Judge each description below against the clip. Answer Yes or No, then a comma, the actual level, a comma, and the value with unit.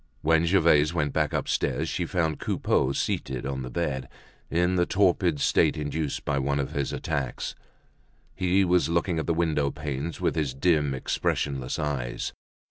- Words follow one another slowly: No, average, 160 wpm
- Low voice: Yes, very low, 75 Hz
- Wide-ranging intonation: No, average, 3.5 semitones